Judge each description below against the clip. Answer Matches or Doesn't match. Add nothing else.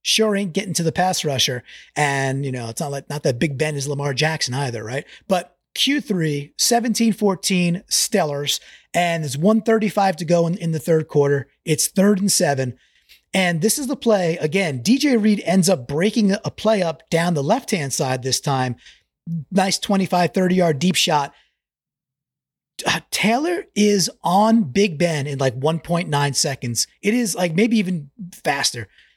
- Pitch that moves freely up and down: Matches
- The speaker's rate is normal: Matches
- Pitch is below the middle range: Doesn't match